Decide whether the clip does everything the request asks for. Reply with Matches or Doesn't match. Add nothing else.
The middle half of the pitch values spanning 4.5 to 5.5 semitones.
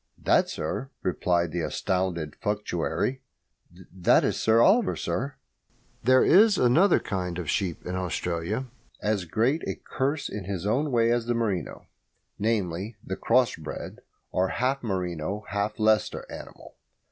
Matches